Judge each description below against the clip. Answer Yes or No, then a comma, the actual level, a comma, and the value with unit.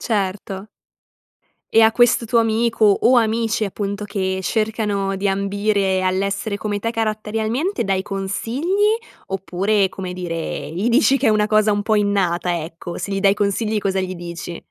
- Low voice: No, high, 205 Hz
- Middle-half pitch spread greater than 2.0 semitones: Yes, narrow, 2.4 semitones